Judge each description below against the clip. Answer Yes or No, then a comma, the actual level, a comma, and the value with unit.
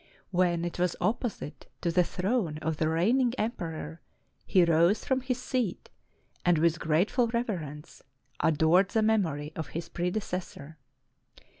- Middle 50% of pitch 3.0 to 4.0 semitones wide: No, average, 5.2 semitones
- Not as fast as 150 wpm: Yes, slow, 135 wpm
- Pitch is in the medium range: Yes, medium, 175 Hz